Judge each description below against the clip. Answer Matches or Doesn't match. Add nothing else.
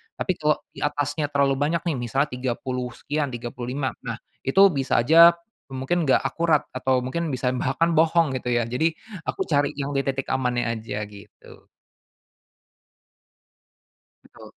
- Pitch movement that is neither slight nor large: Matches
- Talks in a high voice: Doesn't match